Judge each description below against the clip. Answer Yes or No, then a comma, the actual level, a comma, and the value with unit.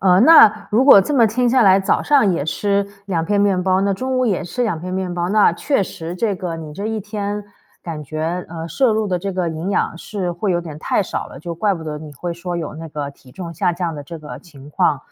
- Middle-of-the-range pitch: Yes, medium, 180 Hz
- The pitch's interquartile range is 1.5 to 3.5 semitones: No, average, 3.9 semitones